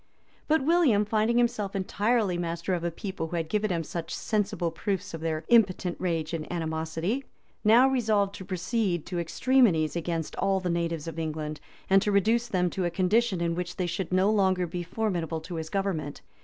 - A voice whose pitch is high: No, medium, 180 Hz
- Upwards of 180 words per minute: Yes, average, 190 wpm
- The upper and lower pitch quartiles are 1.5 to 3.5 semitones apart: No, average, 4.0 semitones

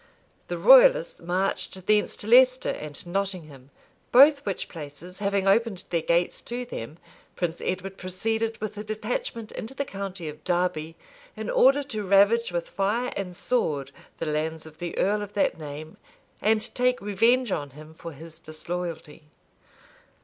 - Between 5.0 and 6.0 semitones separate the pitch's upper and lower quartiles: Yes, wide, 5.6 semitones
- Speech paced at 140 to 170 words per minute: Yes, average, 155 wpm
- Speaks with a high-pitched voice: Yes, high, 195 Hz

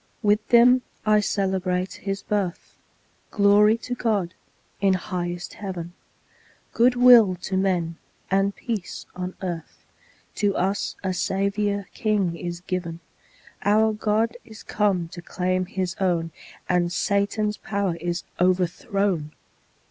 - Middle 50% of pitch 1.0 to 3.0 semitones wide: Yes, average, 2.7 semitones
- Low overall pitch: No, high, 195 Hz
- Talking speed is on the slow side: Yes, slow, 120 wpm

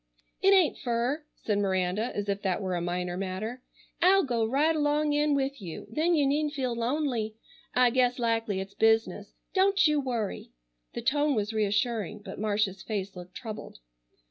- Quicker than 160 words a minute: Yes, average, 170 wpm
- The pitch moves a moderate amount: No, wide, 6.2 semitones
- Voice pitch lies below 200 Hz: No, high, 230 Hz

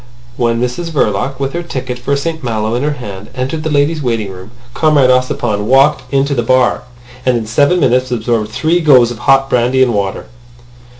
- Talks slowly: No, average, 190 wpm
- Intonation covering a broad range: No, average, 3.2 semitones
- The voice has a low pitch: Yes, low, 130 Hz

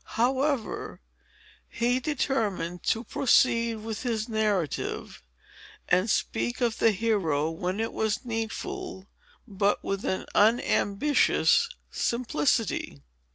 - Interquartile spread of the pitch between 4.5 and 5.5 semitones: No, average, 3.7 semitones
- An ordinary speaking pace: No, slow, 100 wpm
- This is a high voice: Yes, high, 225 Hz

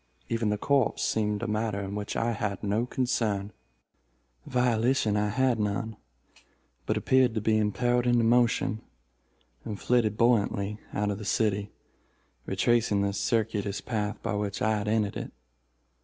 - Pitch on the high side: No, low, 110 Hz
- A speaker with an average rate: Yes, average, 150 wpm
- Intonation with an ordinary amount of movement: No, narrow, 2.3 semitones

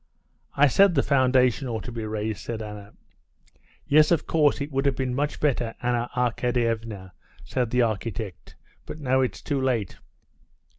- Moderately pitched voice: No, low, 125 Hz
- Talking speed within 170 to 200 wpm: No, average, 160 wpm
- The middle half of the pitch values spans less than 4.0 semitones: Yes, average, 3.5 semitones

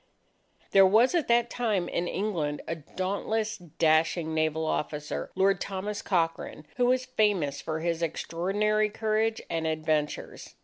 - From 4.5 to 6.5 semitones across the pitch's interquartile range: Yes, average, 5.1 semitones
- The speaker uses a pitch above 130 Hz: Yes, medium, 185 Hz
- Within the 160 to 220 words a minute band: No, slow, 135 wpm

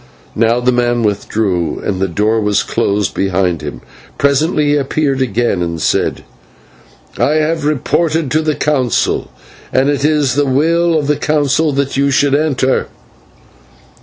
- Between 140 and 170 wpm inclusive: Yes, average, 150 wpm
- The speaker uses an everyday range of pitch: No, wide, 6.1 semitones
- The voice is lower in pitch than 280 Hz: Yes, low, 135 Hz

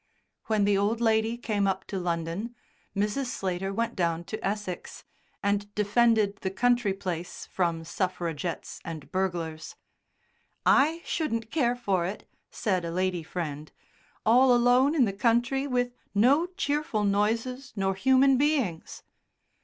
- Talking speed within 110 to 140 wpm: Yes, slow, 135 wpm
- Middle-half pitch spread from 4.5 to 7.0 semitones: Yes, average, 4.8 semitones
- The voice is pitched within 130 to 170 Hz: No, high, 205 Hz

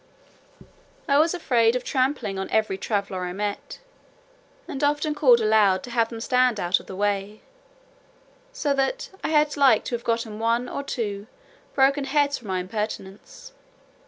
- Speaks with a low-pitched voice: No, high, 230 Hz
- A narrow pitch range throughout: No, average, 5.3 semitones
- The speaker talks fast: No, average, 160 wpm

